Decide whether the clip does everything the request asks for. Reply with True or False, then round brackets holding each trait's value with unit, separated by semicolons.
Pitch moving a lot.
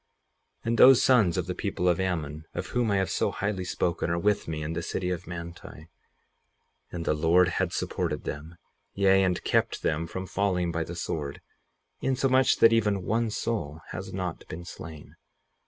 False (3.4 semitones)